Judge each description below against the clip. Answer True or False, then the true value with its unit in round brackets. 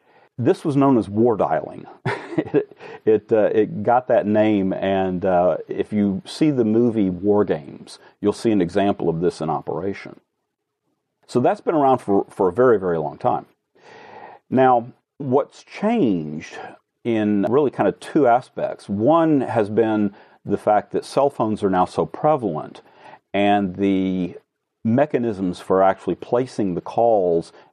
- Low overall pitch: True (105 Hz)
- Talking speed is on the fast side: False (155 wpm)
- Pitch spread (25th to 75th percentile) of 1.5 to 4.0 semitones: False (4.4 semitones)